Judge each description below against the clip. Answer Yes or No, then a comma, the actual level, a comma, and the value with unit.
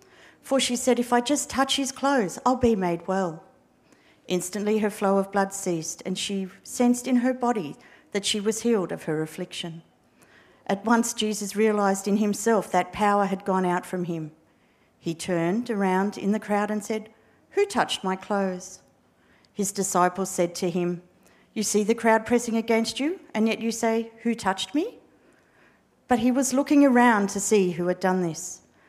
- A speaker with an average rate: Yes, average, 180 wpm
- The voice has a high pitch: Yes, high, 205 Hz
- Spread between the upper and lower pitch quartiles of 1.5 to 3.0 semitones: No, average, 4.0 semitones